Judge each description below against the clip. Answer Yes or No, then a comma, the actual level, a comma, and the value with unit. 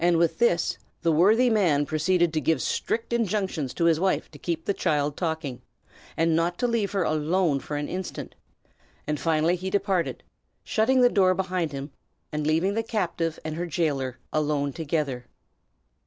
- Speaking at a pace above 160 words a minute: Yes, average, 170 wpm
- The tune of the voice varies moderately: Yes, average, 3.7 semitones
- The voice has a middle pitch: Yes, medium, 170 Hz